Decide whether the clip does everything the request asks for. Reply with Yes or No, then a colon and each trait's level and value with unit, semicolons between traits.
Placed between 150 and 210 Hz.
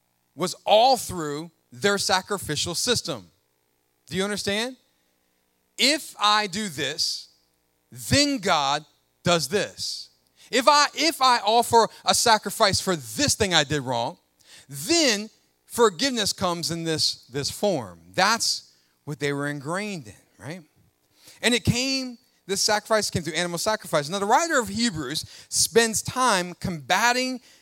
Yes: medium, 185 Hz